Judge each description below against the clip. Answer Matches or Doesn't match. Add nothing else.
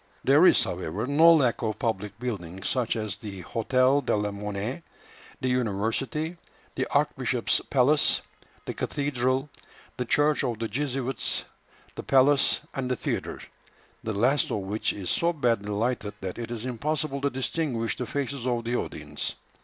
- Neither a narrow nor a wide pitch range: Matches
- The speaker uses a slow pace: Doesn't match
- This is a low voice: Matches